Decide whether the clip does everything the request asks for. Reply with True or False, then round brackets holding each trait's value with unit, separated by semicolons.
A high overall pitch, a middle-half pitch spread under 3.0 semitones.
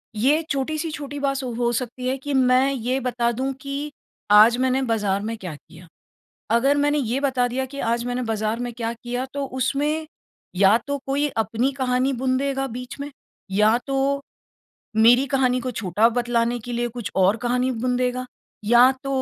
True (250 Hz; 2.6 semitones)